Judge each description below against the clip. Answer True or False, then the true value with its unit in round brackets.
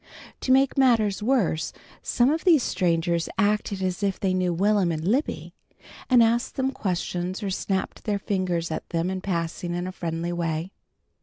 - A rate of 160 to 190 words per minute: True (170 wpm)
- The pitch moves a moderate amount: True (4.3 semitones)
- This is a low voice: False (190 Hz)